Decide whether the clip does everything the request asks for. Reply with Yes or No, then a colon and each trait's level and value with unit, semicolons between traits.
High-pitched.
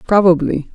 No: medium, 180 Hz